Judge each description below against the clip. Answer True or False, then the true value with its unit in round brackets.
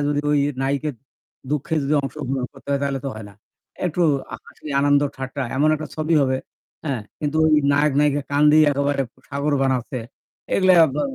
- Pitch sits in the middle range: True (145 Hz)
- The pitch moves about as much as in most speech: False (1.8 semitones)